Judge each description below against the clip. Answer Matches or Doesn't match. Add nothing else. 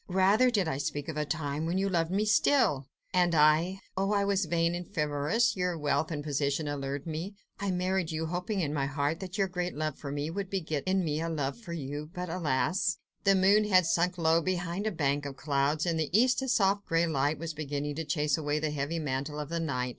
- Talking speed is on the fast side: Matches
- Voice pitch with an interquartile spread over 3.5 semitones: Matches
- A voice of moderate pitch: Matches